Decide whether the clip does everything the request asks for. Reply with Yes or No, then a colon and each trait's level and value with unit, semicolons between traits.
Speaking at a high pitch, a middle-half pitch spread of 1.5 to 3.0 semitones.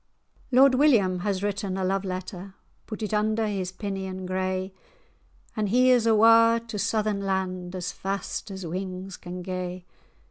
Yes: high, 195 Hz; narrow, 2.6 semitones